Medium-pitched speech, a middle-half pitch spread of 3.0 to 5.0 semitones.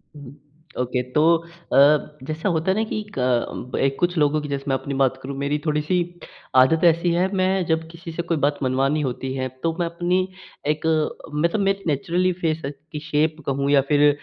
Yes: medium, 150 Hz; average, 3.5 semitones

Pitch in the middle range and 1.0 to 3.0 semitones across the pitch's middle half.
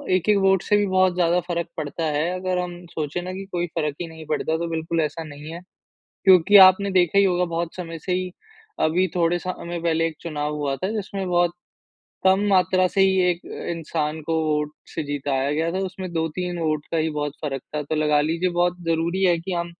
Yes: medium, 170 Hz; average, 2.7 semitones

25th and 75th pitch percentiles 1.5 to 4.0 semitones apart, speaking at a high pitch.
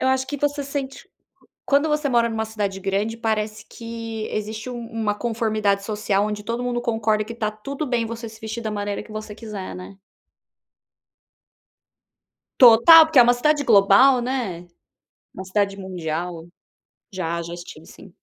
Yes: average, 3.1 semitones; high, 220 Hz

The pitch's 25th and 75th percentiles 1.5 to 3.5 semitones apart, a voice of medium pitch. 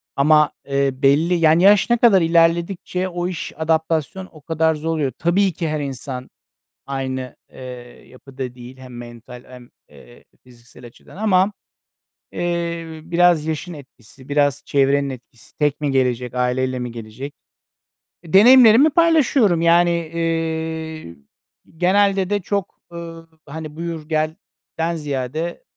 No: average, 4.4 semitones; medium, 160 Hz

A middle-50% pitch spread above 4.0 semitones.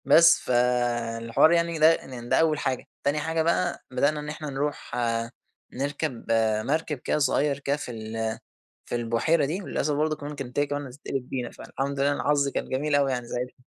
No: average, 3.5 semitones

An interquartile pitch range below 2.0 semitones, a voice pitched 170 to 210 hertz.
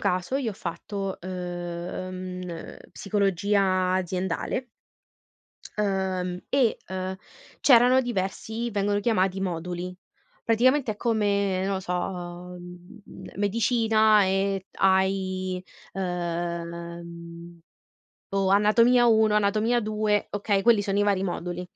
No: average, 2.8 semitones; high, 190 Hz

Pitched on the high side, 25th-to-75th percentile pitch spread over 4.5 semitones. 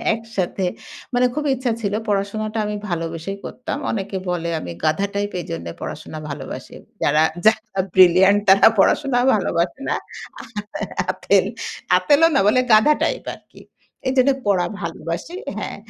Yes: high, 200 Hz; average, 4.9 semitones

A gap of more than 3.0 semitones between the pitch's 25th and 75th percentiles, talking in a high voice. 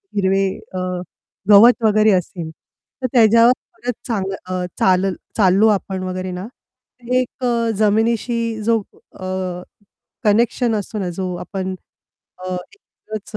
Yes: average, 3.6 semitones; high, 210 Hz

